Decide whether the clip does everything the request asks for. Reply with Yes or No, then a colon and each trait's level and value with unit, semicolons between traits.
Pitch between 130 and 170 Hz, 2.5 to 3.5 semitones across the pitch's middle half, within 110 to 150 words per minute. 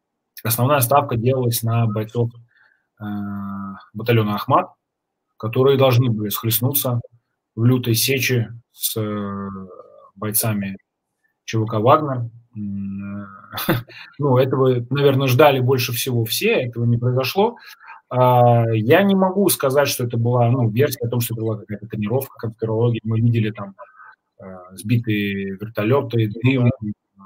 No: low, 115 Hz; average, 3.2 semitones; average, 115 wpm